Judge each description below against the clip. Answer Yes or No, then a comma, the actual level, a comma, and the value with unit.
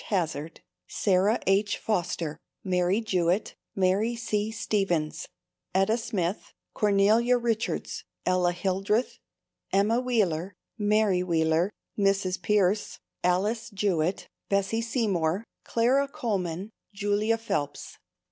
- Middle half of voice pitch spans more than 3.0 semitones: Yes, average, 3.5 semitones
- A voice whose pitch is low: No, high, 200 Hz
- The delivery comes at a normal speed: No, slow, 95 wpm